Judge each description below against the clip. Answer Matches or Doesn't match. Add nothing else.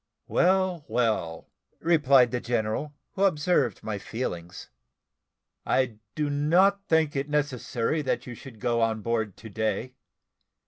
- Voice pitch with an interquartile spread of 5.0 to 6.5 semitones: Matches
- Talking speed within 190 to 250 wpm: Doesn't match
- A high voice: Doesn't match